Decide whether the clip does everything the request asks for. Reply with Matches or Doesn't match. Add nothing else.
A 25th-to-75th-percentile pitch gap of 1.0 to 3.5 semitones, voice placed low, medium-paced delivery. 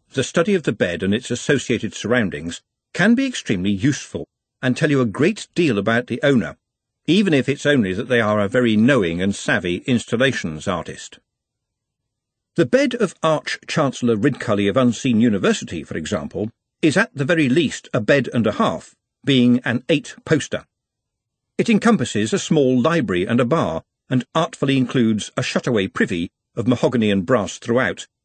Doesn't match